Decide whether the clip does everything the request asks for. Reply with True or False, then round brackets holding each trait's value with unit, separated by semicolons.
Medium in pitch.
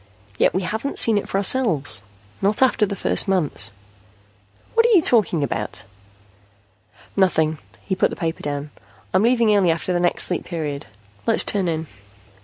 True (180 Hz)